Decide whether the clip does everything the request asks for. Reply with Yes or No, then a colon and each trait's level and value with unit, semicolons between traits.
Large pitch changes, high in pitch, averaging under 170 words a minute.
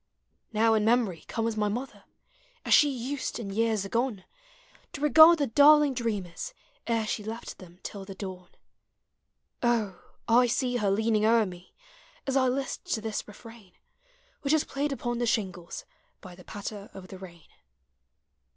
No: average, 4.2 semitones; high, 225 Hz; average, 160 wpm